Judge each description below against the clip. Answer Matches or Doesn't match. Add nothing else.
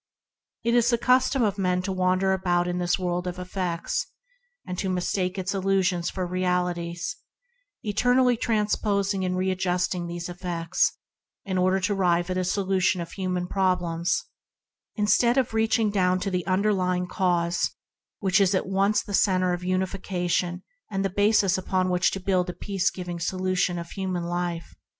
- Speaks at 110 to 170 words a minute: Matches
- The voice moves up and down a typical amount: Doesn't match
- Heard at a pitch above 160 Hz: Matches